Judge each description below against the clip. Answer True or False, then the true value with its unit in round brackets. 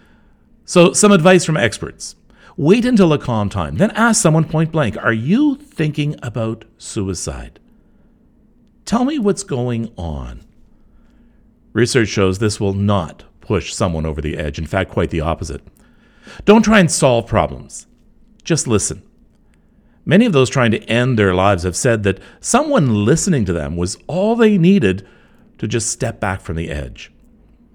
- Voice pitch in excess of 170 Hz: False (115 Hz)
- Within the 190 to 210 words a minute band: False (160 wpm)